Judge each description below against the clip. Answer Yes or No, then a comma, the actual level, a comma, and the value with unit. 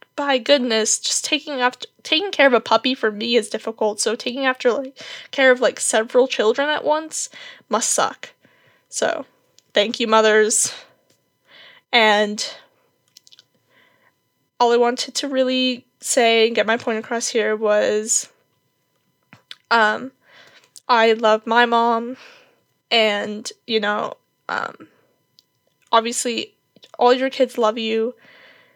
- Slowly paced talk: Yes, slow, 125 wpm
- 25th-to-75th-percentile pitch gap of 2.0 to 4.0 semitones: Yes, average, 3.5 semitones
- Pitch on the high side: Yes, high, 240 Hz